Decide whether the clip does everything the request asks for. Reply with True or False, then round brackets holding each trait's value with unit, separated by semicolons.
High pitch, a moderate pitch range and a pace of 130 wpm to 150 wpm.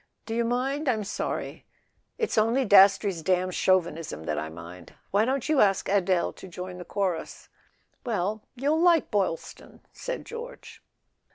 False (200 Hz; 6.0 semitones; 145 wpm)